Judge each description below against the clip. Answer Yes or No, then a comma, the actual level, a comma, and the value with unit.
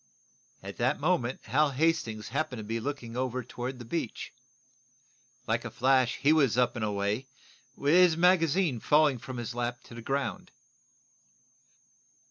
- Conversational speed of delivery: Yes, average, 145 wpm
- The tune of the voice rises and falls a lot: No, average, 4.1 semitones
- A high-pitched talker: No, low, 130 Hz